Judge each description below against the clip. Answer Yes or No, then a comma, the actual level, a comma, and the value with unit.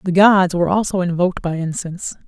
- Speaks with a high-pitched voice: No, medium, 180 Hz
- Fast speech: No, average, 185 wpm